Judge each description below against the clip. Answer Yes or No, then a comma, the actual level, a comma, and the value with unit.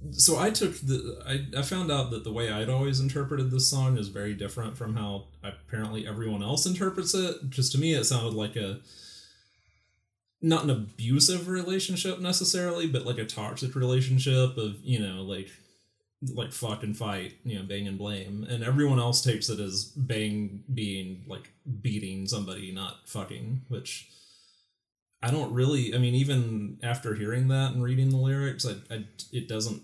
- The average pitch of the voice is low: Yes, low, 120 Hz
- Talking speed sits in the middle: Yes, average, 175 wpm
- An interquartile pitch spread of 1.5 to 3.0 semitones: No, average, 4.2 semitones